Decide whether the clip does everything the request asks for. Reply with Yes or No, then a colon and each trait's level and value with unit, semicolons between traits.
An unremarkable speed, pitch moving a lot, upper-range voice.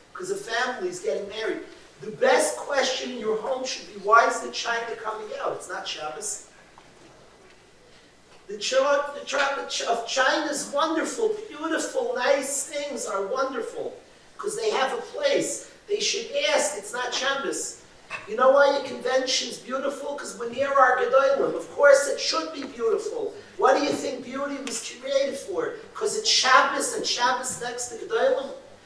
Yes: average, 165 wpm; wide, 8.5 semitones; very high, 275 Hz